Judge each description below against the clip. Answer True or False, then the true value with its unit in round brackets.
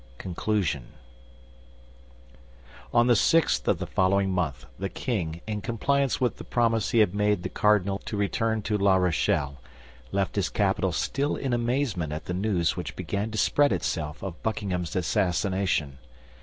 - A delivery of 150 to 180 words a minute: True (155 wpm)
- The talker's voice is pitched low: True (100 Hz)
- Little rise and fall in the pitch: False (4.1 semitones)